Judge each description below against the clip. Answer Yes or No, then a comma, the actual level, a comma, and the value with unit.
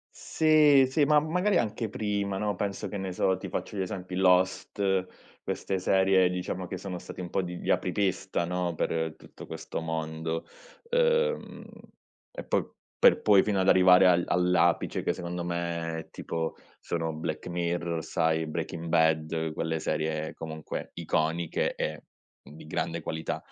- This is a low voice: Yes, very low, 90 Hz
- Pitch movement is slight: No, average, 3.1 semitones